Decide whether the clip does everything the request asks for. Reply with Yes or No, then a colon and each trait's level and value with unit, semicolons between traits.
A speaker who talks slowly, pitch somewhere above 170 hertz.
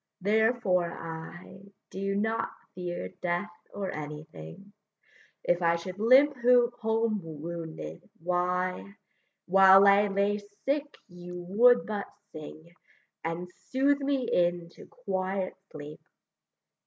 Yes: slow, 105 wpm; high, 190 Hz